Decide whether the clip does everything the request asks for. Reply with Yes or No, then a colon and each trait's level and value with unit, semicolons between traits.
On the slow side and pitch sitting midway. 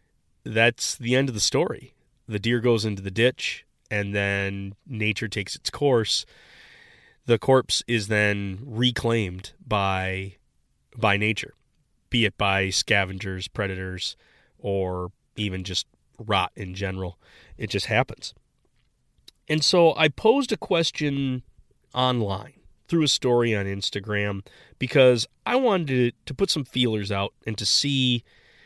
No: slow, 130 wpm; low, 110 Hz